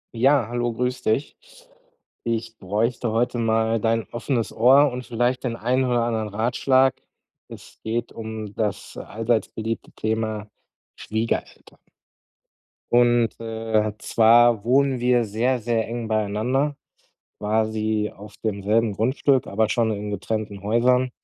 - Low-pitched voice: Yes, low, 115 Hz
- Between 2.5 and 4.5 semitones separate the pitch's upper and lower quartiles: No, narrow, 1.9 semitones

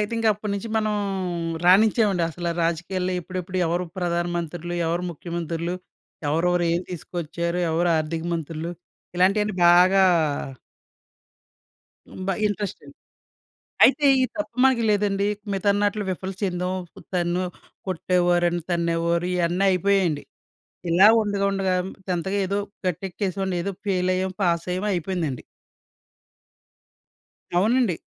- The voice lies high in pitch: No, medium, 180 Hz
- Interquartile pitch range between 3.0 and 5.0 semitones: No, narrow, 2.5 semitones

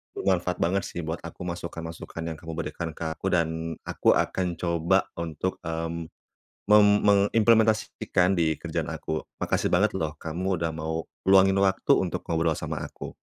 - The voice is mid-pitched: No, very low, 85 Hz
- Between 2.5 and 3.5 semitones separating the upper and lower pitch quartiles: Yes, average, 2.8 semitones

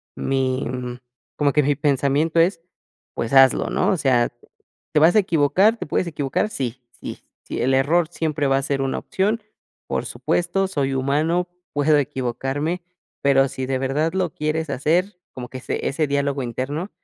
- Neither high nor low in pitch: Yes, medium, 145 Hz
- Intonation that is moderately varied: Yes, average, 3.6 semitones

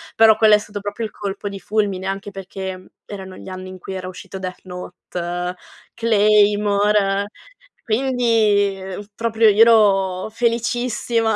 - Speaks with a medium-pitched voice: No, high, 205 Hz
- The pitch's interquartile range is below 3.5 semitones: Yes, narrow, 2.5 semitones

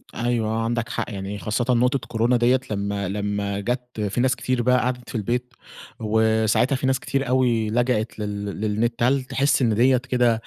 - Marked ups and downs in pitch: No, average, 2.7 semitones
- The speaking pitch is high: No, low, 120 Hz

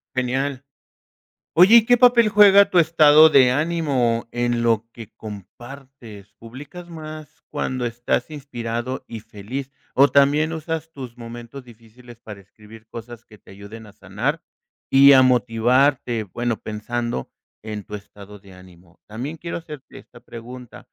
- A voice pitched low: Yes, low, 120 Hz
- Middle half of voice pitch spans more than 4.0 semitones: Yes, average, 4.5 semitones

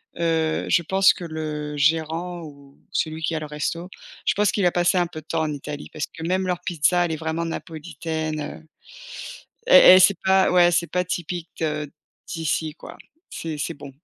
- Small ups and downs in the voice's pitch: Yes, narrow, 2.3 semitones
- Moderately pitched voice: Yes, medium, 160 Hz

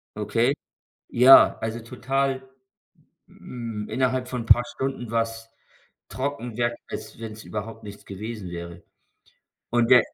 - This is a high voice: No, low, 115 Hz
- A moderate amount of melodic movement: No, narrow, 2.3 semitones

